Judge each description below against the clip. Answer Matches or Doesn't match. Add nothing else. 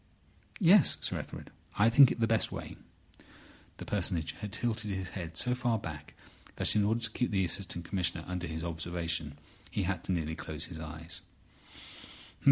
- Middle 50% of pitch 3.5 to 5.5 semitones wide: Matches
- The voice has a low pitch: Matches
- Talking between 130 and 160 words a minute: Doesn't match